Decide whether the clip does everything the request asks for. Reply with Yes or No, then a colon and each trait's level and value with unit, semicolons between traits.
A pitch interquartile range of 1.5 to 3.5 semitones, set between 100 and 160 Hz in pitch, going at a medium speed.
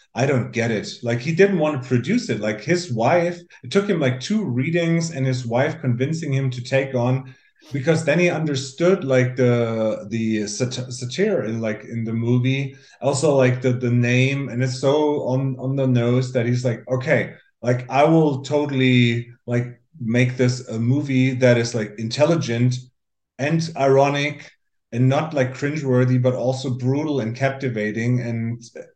Yes: average, 2.8 semitones; low, 130 Hz; average, 170 wpm